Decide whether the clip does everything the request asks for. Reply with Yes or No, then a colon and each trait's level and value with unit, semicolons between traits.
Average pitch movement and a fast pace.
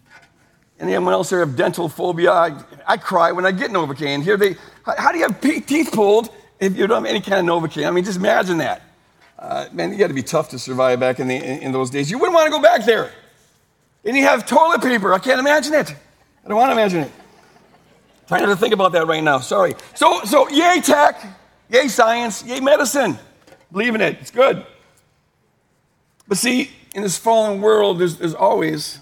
No: wide, 8.3 semitones; fast, 215 wpm